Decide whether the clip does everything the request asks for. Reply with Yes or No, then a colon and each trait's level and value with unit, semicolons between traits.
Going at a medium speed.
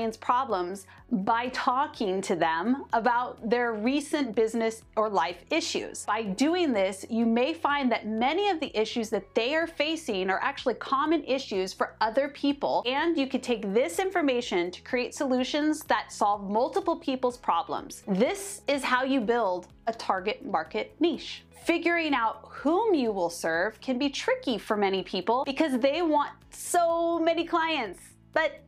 Yes: average, 160 wpm